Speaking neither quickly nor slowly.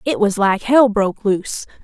Yes: average, 195 wpm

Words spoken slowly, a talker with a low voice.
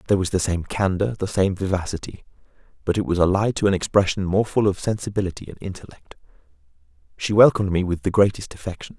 No: average, 185 wpm; very low, 95 Hz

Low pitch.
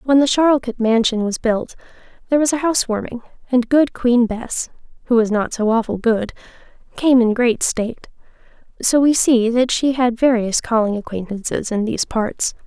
No: high, 240 Hz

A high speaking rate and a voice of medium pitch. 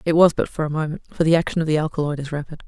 Yes: fast, 315 wpm; medium, 155 Hz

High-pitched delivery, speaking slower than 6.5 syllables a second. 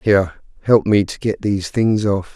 No: low, 105 Hz; 5.0 syllables/s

